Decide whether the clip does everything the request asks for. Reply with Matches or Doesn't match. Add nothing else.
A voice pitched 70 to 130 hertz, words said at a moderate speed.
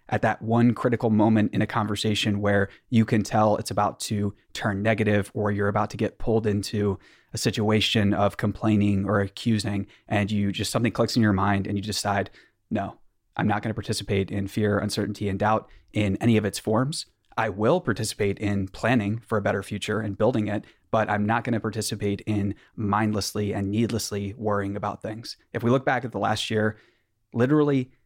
Matches